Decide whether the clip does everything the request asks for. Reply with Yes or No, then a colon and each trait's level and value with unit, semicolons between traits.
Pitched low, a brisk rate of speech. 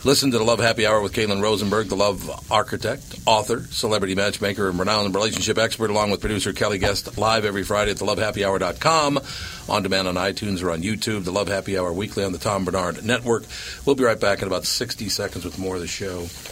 Yes: low, 100 Hz; fast, 215 wpm